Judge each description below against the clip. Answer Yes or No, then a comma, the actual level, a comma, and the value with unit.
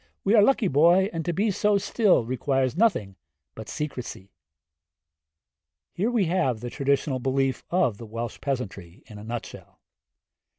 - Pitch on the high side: No, low, 135 Hz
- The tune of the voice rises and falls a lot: Yes, wide, 8.0 semitones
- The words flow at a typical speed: Yes, average, 155 wpm